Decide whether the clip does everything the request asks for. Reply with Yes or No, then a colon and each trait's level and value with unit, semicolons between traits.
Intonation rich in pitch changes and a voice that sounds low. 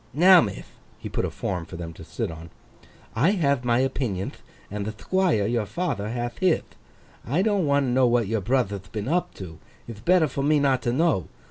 Yes: wide, 7.0 semitones; low, 120 Hz